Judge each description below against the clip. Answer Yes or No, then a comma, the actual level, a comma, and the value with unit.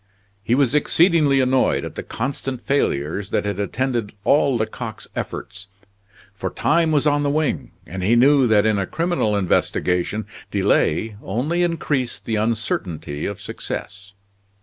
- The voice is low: Yes, low, 120 Hz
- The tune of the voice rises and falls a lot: Yes, wide, 5.9 semitones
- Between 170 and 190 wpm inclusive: No, average, 145 wpm